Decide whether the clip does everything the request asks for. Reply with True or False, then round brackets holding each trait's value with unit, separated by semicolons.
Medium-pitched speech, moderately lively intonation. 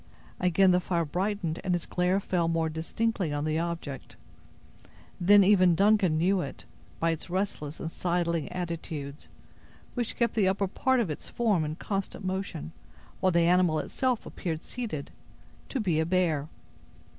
True (180 Hz; 3.3 semitones)